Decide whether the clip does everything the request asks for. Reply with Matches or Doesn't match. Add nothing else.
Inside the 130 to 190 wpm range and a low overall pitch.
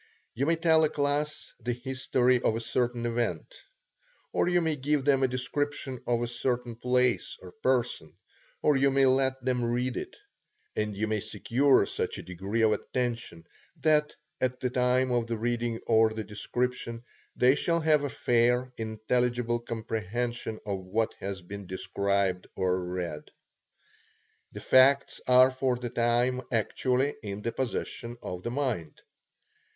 Matches